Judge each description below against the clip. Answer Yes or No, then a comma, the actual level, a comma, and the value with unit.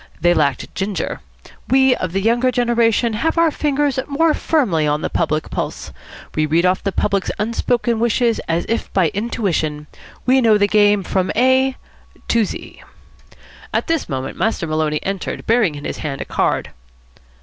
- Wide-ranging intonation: Yes, wide, 6.5 semitones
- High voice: Yes, high, 210 Hz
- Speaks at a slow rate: No, average, 165 wpm